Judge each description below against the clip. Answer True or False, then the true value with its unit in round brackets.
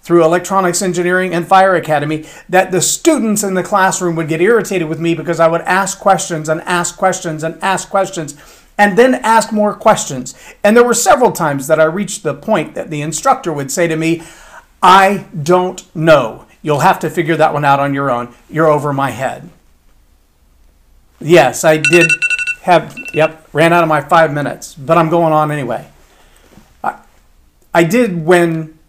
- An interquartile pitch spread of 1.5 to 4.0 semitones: True (3.7 semitones)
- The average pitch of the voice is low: False (165 Hz)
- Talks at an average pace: True (180 wpm)